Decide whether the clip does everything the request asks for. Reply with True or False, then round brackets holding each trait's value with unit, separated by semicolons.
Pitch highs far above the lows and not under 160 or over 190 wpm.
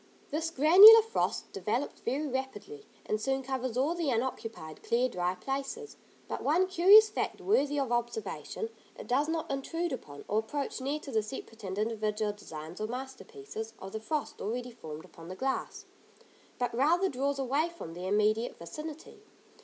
True (6.0 semitones; 165 wpm)